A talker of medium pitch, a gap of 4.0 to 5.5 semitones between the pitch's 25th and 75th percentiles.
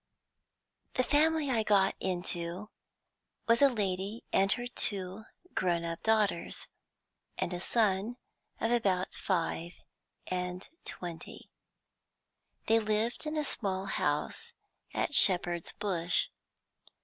No: high, 195 Hz; average, 4.3 semitones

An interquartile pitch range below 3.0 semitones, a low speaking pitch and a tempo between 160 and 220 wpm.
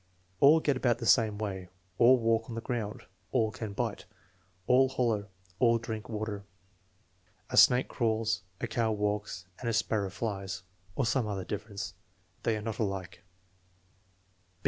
No: narrow, 2.4 semitones; low, 110 Hz; average, 150 wpm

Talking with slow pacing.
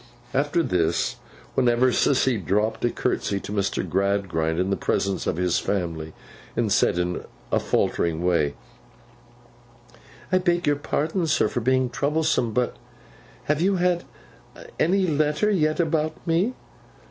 Yes: slow, 130 wpm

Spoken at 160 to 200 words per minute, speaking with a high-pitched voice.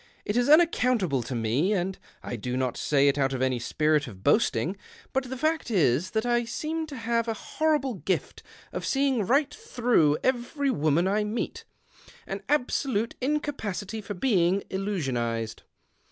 Yes: average, 165 wpm; high, 205 Hz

